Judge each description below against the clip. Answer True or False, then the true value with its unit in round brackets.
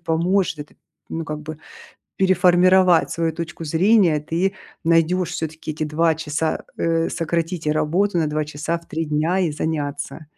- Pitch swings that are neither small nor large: False (2.3 semitones)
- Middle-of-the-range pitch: True (165 Hz)